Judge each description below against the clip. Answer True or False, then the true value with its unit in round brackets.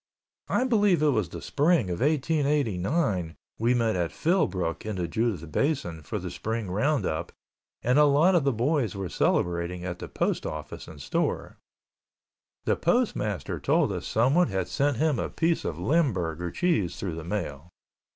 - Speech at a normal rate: True (165 wpm)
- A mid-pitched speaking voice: False (110 Hz)